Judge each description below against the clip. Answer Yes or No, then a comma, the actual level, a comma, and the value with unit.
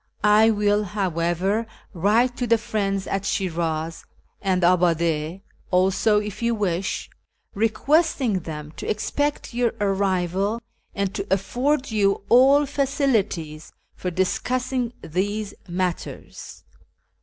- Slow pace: Yes, slow, 115 wpm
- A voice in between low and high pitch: No, high, 200 Hz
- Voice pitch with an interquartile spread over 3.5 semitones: Yes, average, 4.1 semitones